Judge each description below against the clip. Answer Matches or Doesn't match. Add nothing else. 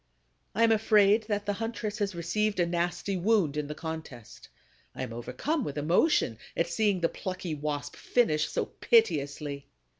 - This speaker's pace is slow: Doesn't match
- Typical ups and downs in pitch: Doesn't match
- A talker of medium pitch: Matches